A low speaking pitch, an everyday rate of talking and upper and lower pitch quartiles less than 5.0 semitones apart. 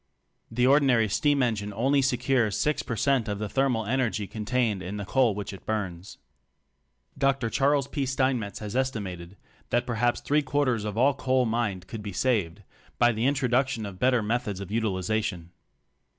Yes: low, 115 Hz; average, 165 wpm; average, 4.1 semitones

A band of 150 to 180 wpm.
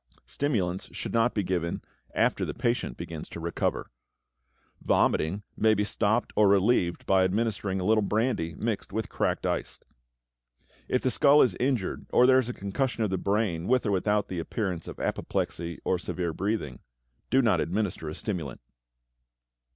Yes: average, 160 wpm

